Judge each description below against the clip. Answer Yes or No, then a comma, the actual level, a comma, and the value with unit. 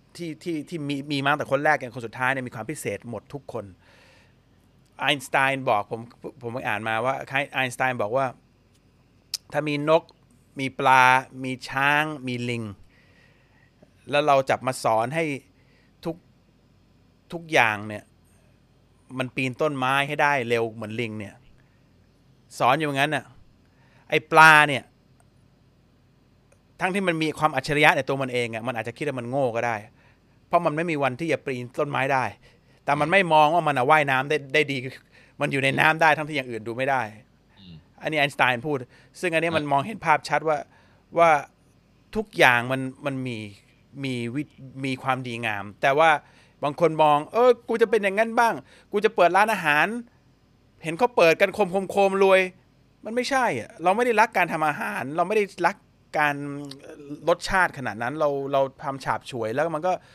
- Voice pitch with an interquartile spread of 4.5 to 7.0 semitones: No, average, 3.8 semitones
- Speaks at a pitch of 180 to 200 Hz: No, low, 135 Hz